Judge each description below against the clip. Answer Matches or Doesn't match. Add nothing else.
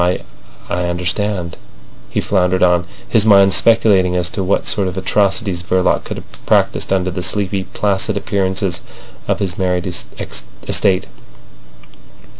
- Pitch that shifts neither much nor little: Doesn't match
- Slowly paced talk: Matches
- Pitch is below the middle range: Matches